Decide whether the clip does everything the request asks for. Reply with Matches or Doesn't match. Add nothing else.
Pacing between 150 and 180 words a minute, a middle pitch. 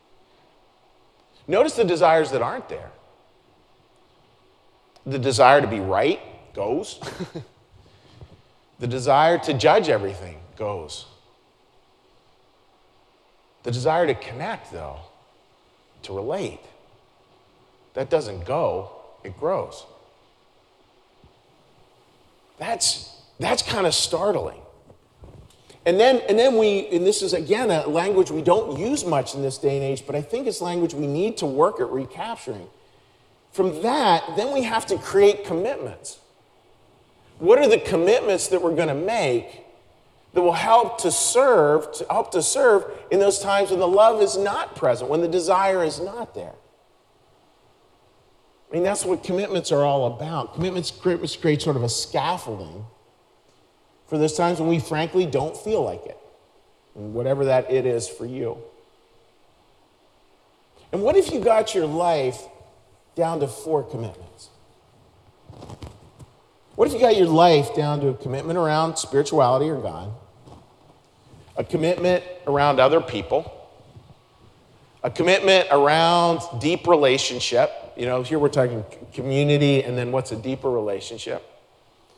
Doesn't match